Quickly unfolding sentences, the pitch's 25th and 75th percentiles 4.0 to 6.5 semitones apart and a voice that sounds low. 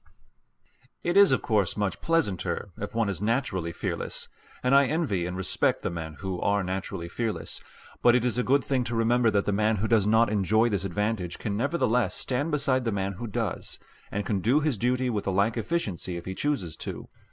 Yes: fast, 210 wpm; average, 4.4 semitones; low, 110 Hz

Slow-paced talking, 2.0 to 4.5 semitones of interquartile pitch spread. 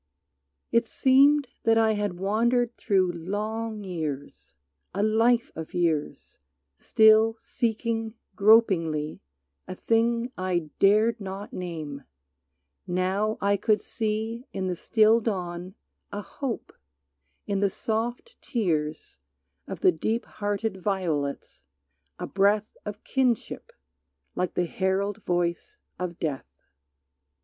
Yes: slow, 110 wpm; average, 4.0 semitones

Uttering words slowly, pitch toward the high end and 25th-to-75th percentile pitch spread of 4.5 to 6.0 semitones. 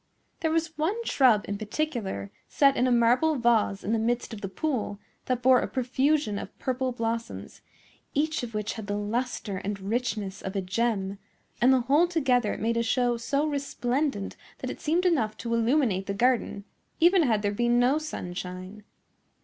No: average, 180 wpm; high, 240 Hz; average, 4.9 semitones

